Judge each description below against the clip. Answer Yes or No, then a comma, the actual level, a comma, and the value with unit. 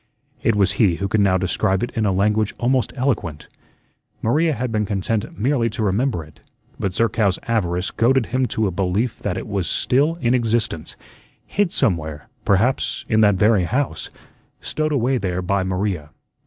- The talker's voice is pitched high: No, low, 105 Hz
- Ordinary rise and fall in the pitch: Yes, average, 4.6 semitones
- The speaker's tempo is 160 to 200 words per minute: Yes, average, 170 wpm